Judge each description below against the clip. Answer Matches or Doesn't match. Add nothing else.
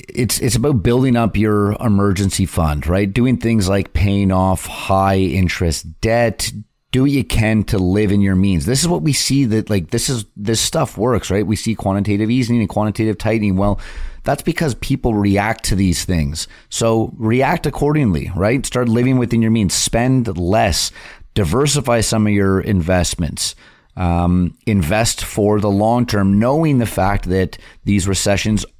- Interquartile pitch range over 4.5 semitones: Doesn't match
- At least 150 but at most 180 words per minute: Matches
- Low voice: Matches